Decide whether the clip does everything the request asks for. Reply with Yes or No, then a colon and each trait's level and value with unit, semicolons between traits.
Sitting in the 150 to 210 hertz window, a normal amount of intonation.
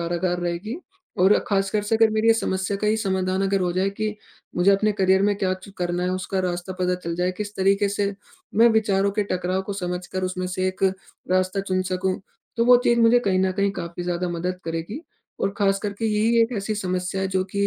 No: high, 190 Hz; narrow, 2.0 semitones